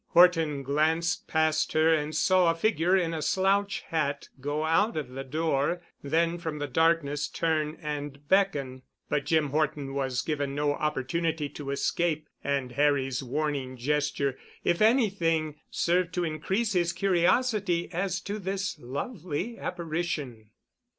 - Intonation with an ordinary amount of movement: Yes, average, 3.4 semitones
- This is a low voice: No, medium, 155 Hz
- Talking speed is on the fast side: No, average, 140 wpm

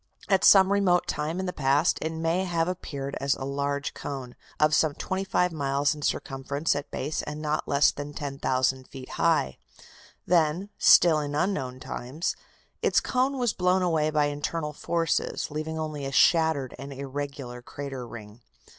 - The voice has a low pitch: No, medium, 150 Hz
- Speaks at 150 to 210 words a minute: Yes, average, 165 wpm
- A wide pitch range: No, average, 3.3 semitones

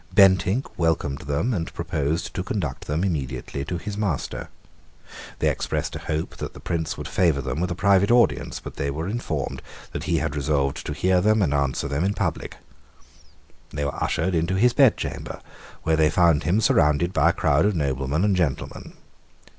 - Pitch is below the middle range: Yes, very low, 80 Hz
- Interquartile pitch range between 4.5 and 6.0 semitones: Yes, average, 4.8 semitones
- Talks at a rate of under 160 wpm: No, average, 185 wpm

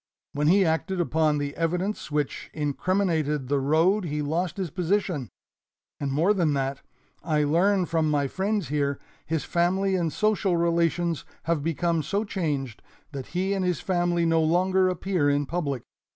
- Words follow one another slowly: No, average, 160 wpm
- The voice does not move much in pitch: No, average, 3.9 semitones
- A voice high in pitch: No, medium, 165 Hz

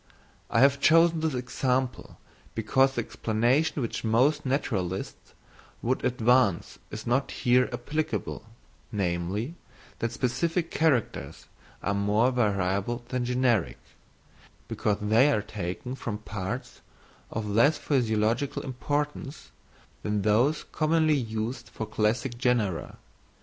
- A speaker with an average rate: No, slow, 110 wpm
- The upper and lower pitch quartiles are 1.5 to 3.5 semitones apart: No, average, 4.1 semitones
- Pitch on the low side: Yes, low, 120 Hz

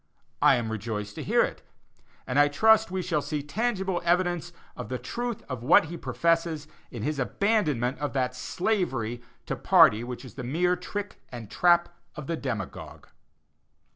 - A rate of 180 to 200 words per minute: No, average, 170 wpm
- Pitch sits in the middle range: Yes, medium, 150 Hz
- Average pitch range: No, wide, 6.4 semitones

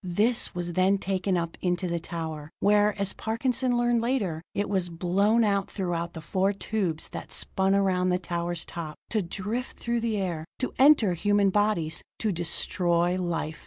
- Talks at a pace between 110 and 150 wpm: No, average, 170 wpm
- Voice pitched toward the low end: No, high, 190 Hz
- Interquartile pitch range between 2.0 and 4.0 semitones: Yes, average, 3.4 semitones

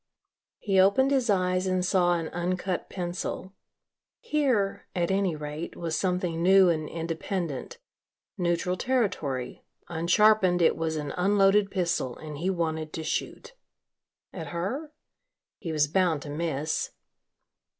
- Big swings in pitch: No, average, 3.2 semitones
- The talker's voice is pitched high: No, medium, 180 Hz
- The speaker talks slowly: Yes, slow, 130 wpm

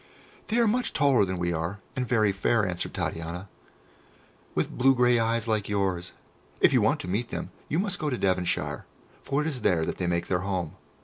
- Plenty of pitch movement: Yes, wide, 5.9 semitones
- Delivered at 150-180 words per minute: No, fast, 205 wpm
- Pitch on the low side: Yes, low, 105 Hz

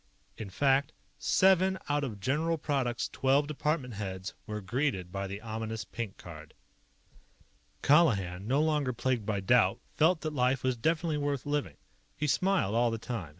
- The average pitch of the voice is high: No, low, 125 Hz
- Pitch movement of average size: No, wide, 5.8 semitones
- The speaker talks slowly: No, average, 155 wpm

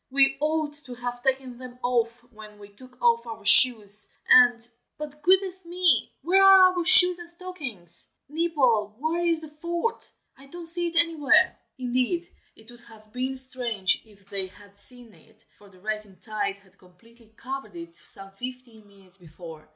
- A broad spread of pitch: Yes, wide, 6.9 semitones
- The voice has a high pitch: Yes, high, 245 Hz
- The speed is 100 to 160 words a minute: No, average, 170 wpm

